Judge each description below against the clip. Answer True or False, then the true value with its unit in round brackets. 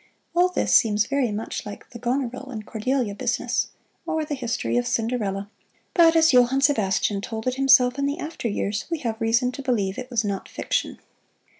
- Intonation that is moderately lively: True (4.3 semitones)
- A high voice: True (245 Hz)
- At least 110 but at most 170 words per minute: False (185 wpm)